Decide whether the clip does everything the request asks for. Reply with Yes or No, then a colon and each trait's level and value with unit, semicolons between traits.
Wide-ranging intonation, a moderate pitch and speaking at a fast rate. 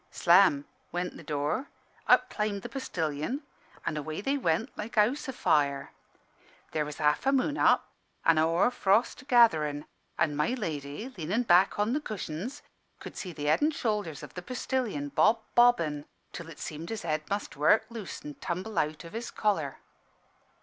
No: wide, 7.1 semitones; medium, 180 Hz; average, 175 wpm